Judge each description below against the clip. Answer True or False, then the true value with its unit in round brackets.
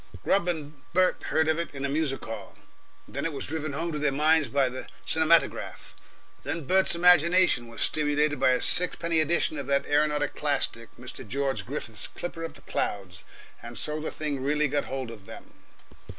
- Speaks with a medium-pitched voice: True (150 Hz)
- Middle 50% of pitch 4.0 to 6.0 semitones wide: False (3.2 semitones)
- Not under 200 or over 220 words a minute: False (185 wpm)